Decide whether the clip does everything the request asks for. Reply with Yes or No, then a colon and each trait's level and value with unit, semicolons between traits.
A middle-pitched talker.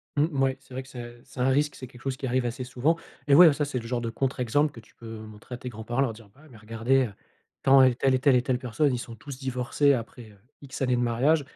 No: low, 130 Hz